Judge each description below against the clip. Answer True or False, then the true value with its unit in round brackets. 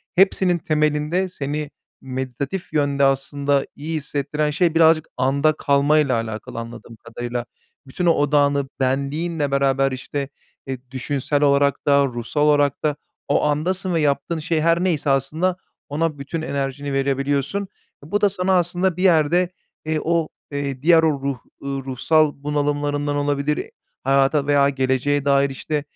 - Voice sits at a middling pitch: True (145 Hz)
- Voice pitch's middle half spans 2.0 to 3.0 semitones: True (2.4 semitones)